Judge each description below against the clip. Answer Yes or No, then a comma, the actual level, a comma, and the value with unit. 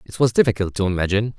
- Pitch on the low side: Yes, low, 105 Hz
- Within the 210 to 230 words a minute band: Yes, fast, 215 wpm